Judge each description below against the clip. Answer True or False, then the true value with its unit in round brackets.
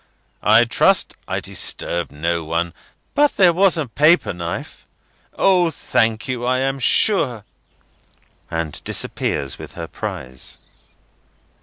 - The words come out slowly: True (115 wpm)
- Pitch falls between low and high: False (120 Hz)